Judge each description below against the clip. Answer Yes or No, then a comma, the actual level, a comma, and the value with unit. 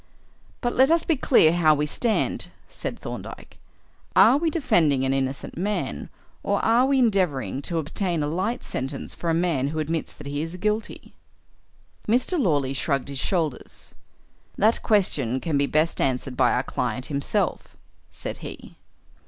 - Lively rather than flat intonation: Yes, wide, 7.4 semitones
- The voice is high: No, medium, 165 Hz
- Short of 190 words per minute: Yes, average, 160 wpm